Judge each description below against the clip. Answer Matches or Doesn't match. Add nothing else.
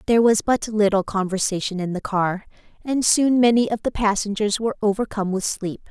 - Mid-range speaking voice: Doesn't match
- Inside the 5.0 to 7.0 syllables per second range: Matches